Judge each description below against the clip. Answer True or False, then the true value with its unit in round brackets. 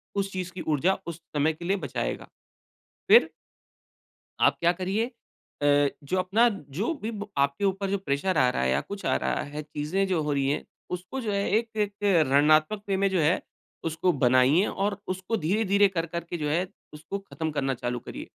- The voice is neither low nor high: True (180 Hz)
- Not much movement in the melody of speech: False (4.9 semitones)